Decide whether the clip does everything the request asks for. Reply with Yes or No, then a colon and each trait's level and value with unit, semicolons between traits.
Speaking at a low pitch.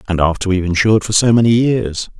Yes: low, 100 Hz